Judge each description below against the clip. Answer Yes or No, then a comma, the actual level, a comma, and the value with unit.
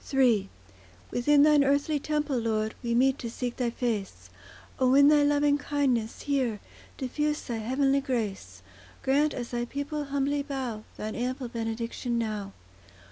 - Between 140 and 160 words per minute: Yes, average, 145 wpm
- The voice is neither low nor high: No, very high, 255 Hz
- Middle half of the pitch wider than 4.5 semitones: No, average, 3.6 semitones